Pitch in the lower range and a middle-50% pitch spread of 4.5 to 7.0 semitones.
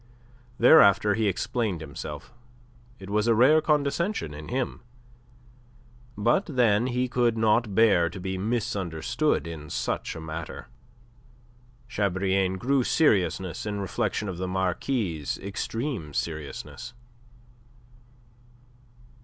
Yes: low, 105 Hz; average, 4.8 semitones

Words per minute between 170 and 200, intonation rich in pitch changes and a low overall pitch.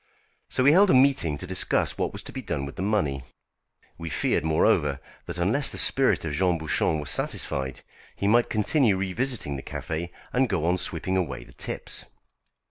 Yes: average, 190 wpm; wide, 7.3 semitones; very low, 90 Hz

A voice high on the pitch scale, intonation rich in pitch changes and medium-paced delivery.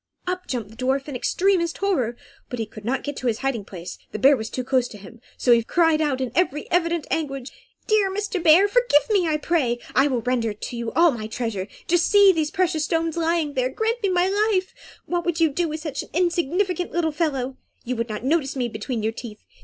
No: very high, 295 Hz; wide, 6.1 semitones; fast, 225 wpm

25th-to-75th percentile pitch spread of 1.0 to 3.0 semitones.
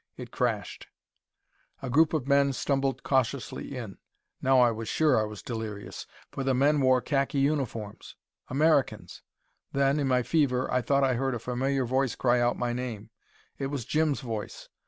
Yes: narrow, 2.4 semitones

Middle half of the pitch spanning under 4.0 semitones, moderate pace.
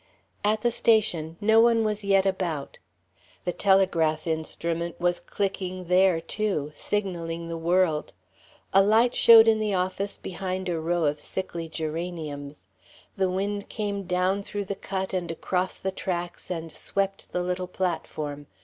Yes: average, 3.0 semitones; average, 150 wpm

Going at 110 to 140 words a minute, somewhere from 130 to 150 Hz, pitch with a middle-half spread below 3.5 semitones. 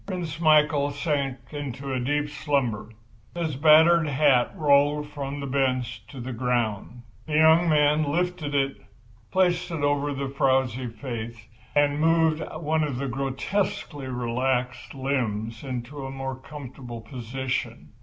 Yes: slow, 135 wpm; medium, 140 Hz; average, 3.1 semitones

